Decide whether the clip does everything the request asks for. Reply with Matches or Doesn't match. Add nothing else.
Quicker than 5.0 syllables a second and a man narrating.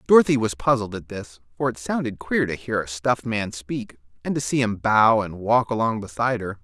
Matches